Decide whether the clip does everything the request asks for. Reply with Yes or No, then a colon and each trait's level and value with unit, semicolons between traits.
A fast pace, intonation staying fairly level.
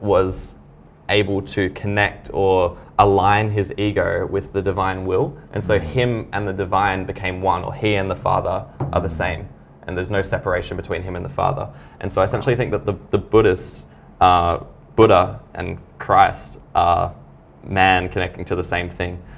No: average, 175 wpm; narrow, 2.3 semitones